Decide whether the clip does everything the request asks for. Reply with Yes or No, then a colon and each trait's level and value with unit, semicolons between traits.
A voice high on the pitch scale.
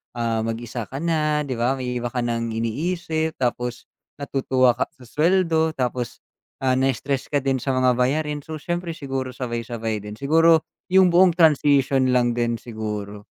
No: low, 130 Hz